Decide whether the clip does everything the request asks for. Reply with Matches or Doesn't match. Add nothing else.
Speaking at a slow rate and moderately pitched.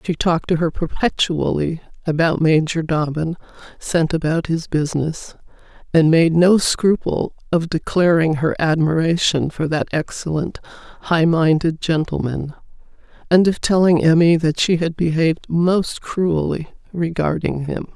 Matches